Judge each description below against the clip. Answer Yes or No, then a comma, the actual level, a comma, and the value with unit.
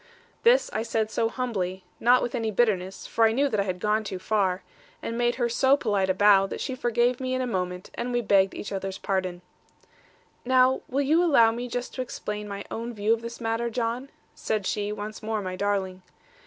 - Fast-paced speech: Yes, fast, 220 wpm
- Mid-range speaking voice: No, high, 220 Hz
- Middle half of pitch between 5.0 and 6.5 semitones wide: No, average, 3.6 semitones